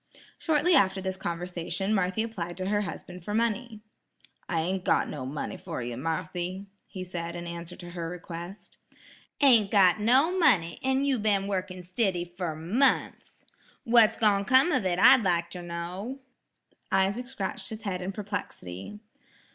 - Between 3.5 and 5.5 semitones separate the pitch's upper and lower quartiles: Yes, average, 3.9 semitones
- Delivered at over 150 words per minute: Yes, average, 160 wpm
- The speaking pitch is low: No, high, 190 Hz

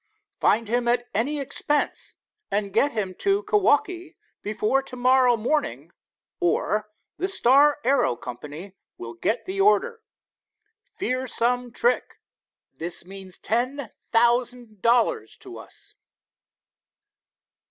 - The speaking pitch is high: Yes, very high, 250 Hz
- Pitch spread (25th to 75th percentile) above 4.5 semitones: Yes, average, 5.1 semitones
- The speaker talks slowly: Yes, slow, 110 wpm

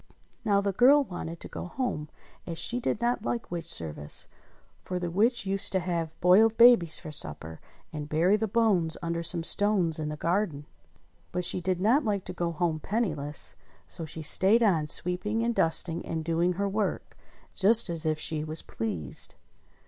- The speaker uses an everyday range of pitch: Yes, average, 4.6 semitones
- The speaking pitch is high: No, medium, 175 Hz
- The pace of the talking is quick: No, average, 180 wpm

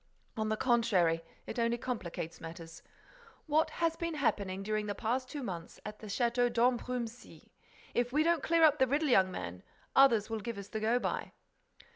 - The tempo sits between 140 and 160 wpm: No, average, 180 wpm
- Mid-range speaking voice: No, high, 235 Hz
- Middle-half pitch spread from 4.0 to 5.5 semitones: Yes, average, 4.4 semitones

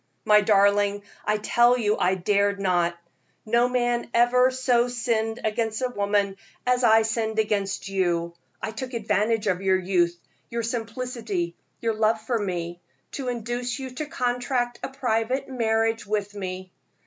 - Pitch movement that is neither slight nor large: Yes, average, 3.2 semitones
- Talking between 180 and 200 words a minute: No, average, 150 wpm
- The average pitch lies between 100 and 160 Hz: No, high, 220 Hz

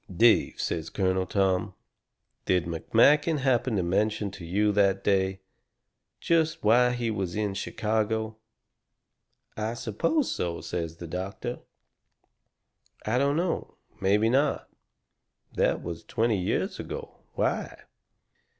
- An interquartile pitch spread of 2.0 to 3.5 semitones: No, average, 4.0 semitones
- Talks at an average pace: No, slow, 115 wpm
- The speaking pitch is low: Yes, low, 105 Hz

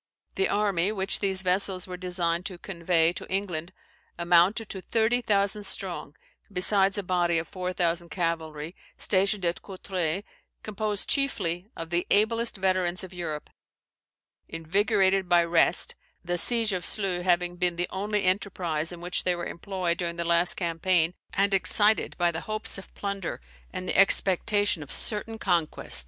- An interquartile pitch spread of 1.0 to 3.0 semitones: Yes, narrow, 2.6 semitones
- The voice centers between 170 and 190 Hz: Yes, medium, 185 Hz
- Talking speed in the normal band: Yes, average, 155 wpm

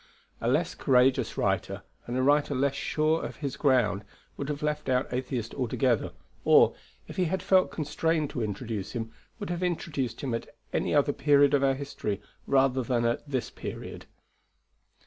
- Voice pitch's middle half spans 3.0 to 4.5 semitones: Yes, average, 3.3 semitones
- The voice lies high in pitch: No, low, 135 Hz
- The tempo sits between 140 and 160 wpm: No, average, 170 wpm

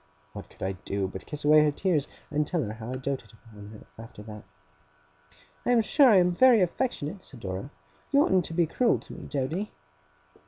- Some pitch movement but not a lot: No, wide, 8.8 semitones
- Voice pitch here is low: No, medium, 150 Hz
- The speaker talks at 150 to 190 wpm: No, fast, 205 wpm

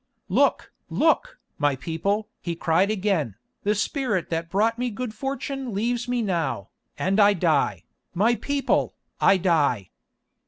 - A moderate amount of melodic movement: No, wide, 6.2 semitones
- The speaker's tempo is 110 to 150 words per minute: Yes, average, 140 wpm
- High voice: Yes, high, 200 Hz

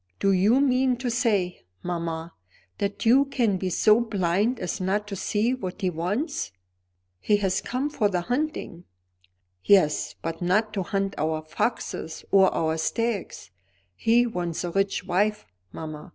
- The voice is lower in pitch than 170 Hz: No, high, 195 Hz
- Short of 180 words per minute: Yes, average, 150 wpm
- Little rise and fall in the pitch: No, average, 4.7 semitones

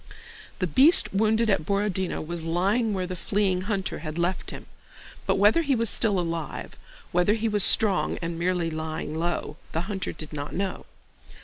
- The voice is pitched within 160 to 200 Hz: Yes, medium, 185 Hz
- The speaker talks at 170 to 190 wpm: Yes, average, 175 wpm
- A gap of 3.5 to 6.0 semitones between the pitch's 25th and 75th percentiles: Yes, average, 3.8 semitones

